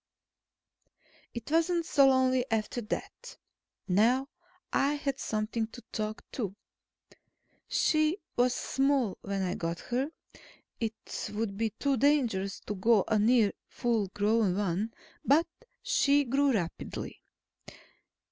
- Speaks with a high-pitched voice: Yes, high, 230 Hz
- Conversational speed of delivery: No, slow, 120 wpm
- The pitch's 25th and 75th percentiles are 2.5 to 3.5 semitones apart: No, average, 4.7 semitones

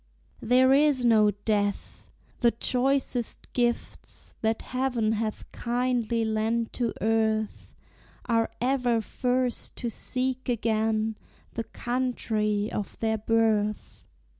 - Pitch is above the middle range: Yes, high, 230 Hz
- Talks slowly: Yes, slow, 105 wpm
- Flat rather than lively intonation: Yes, narrow, 2.3 semitones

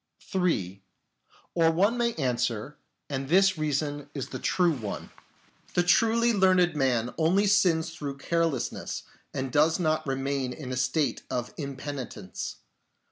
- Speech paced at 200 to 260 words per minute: No, slow, 135 wpm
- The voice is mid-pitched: Yes, medium, 150 Hz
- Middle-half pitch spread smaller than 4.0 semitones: No, average, 5.0 semitones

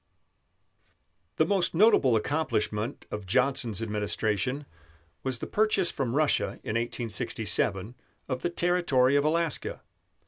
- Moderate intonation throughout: No, wide, 6.2 semitones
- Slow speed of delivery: Yes, slow, 110 wpm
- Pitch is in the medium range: No, low, 130 Hz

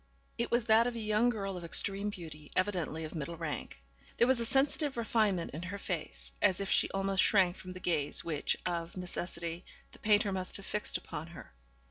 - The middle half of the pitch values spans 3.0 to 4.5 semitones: Yes, average, 3.9 semitones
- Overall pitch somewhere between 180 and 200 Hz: Yes, high, 190 Hz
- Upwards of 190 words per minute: Yes, average, 200 wpm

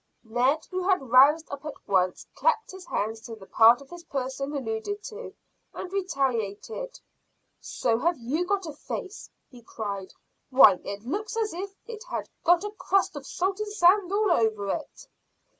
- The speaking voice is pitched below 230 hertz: No, very high, 290 Hz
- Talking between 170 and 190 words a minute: Yes, average, 175 wpm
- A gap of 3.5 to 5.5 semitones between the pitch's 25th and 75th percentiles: No, wide, 9.0 semitones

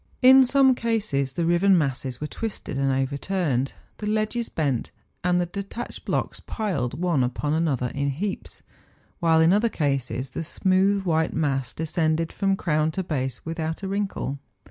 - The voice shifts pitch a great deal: Yes, wide, 6.0 semitones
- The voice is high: No, medium, 165 Hz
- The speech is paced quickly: No, average, 165 wpm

